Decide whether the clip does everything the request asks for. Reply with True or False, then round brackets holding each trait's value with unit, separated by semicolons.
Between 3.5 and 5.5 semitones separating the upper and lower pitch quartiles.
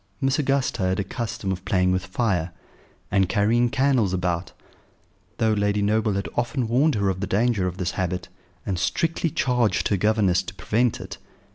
True (4.3 semitones)